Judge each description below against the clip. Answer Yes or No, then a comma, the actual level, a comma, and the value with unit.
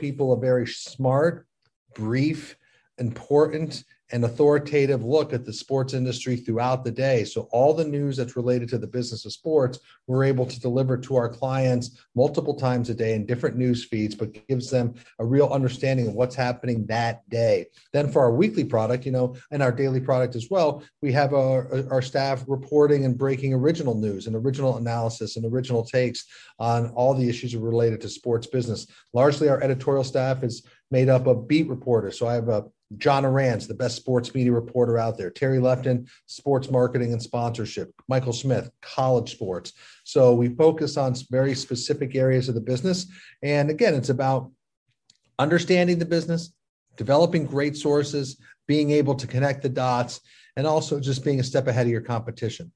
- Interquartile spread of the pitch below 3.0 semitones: Yes, narrow, 2.5 semitones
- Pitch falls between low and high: No, low, 130 Hz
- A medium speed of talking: Yes, average, 180 wpm